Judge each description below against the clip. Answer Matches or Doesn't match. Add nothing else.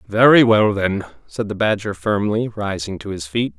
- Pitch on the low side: Matches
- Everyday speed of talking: Matches